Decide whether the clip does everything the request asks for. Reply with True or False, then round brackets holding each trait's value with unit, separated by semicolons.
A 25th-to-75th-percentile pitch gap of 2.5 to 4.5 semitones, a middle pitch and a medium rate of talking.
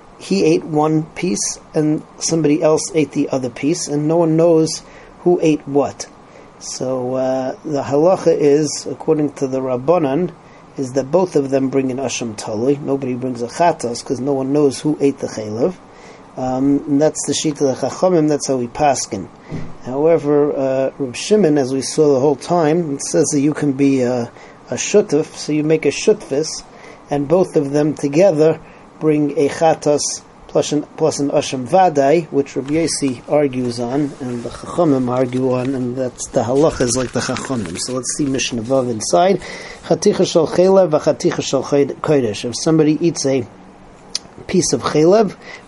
True (3.1 semitones; 145 Hz; 170 wpm)